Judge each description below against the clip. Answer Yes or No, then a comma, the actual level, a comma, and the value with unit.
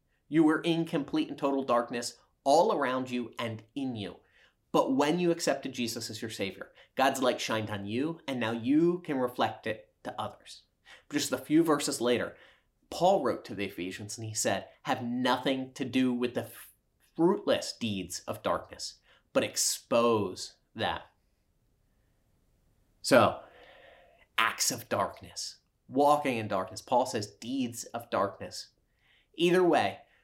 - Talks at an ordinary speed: Yes, average, 150 wpm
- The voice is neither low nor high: No, low, 125 Hz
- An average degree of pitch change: Yes, average, 4.6 semitones